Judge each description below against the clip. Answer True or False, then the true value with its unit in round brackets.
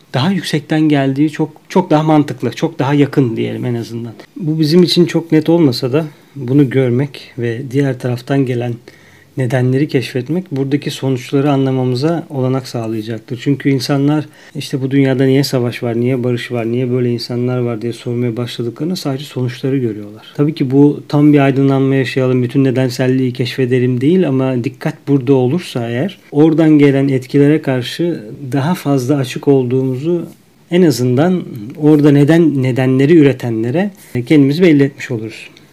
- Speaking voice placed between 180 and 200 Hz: False (135 Hz)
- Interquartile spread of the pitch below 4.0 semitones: True (3.2 semitones)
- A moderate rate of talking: False (150 wpm)